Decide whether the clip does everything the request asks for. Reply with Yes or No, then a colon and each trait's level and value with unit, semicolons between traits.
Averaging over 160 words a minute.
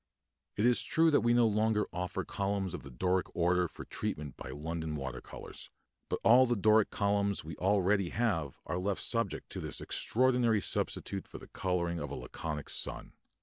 Yes: average, 185 wpm